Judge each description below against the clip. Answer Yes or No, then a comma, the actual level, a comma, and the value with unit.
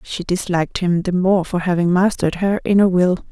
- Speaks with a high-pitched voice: No, medium, 180 Hz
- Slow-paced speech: No, average, 200 wpm